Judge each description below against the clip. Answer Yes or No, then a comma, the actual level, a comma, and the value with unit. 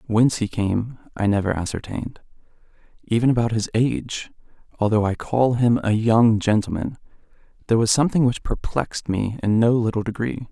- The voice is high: No, low, 115 Hz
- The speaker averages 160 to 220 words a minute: No, average, 145 wpm